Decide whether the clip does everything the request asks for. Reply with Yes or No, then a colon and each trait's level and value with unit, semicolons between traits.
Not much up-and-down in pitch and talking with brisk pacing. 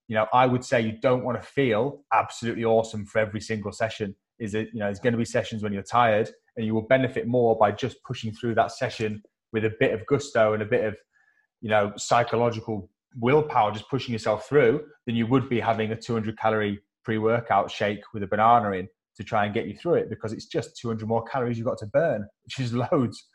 Yes: narrow, 2.1 semitones; fast, 235 wpm